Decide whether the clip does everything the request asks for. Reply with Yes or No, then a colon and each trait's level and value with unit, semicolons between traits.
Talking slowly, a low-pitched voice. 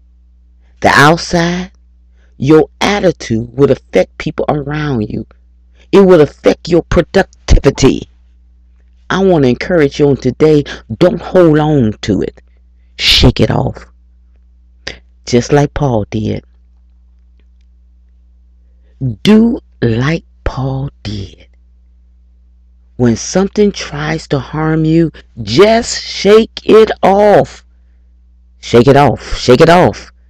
Yes: slow, 105 wpm; low, 110 Hz